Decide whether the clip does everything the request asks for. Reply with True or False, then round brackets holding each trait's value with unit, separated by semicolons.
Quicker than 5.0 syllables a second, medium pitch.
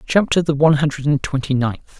True (6.0 syllables/s; 145 Hz)